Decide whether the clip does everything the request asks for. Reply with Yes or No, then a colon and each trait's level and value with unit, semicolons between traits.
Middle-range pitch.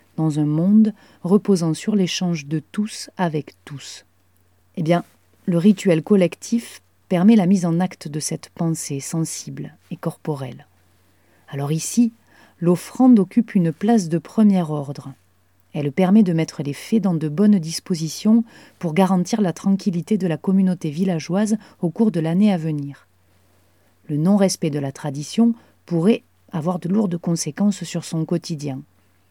Yes: medium, 170 Hz